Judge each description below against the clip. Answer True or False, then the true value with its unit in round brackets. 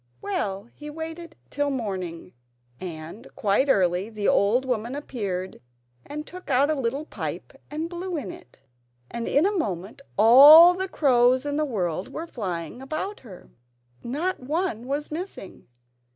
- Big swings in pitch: True (7.3 semitones)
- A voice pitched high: True (260 Hz)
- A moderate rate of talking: True (150 wpm)